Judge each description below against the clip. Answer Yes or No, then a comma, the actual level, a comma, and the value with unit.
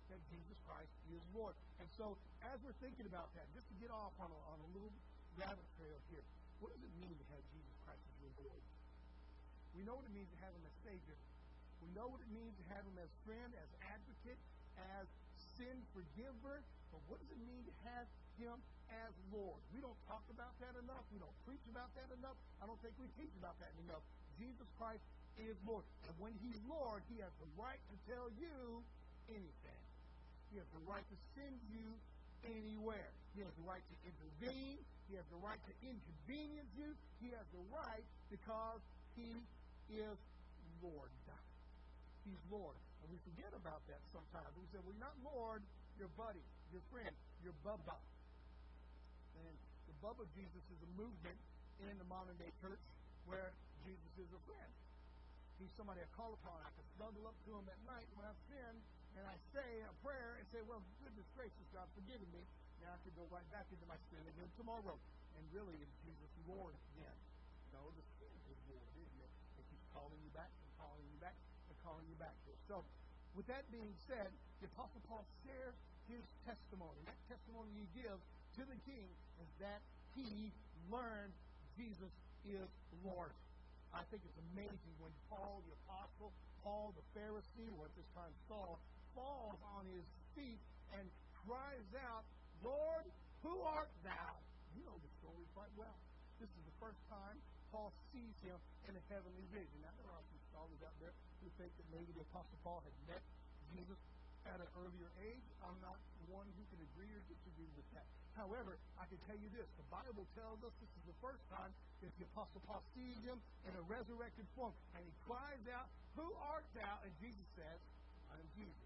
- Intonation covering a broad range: Yes, wide, 6.7 semitones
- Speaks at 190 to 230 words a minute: Yes, average, 195 wpm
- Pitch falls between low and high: No, high, 200 Hz